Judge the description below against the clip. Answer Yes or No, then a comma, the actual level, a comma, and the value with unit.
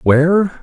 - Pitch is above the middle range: No, medium, 170 Hz